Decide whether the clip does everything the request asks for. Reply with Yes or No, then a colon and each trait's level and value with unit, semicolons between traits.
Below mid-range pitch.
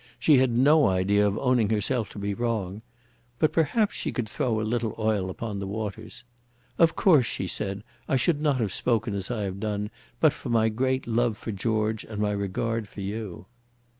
Yes: low, 110 Hz